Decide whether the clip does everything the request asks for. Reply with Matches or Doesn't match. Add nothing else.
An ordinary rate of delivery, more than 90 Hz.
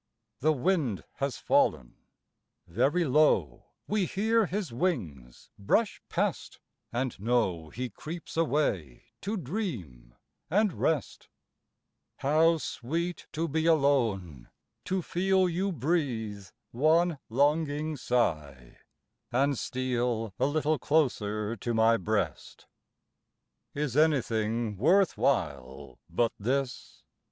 Doesn't match